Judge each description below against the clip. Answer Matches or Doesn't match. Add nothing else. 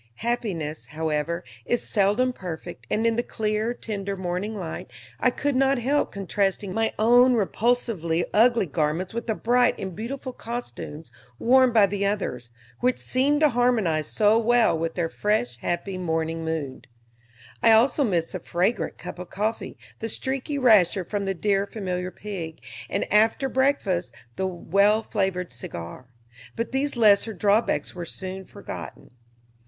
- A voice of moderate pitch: Doesn't match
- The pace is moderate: Matches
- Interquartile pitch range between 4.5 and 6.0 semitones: Matches